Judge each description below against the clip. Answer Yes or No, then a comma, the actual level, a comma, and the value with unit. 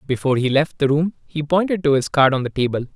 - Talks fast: Yes, fast, 265 wpm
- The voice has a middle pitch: Yes, medium, 150 Hz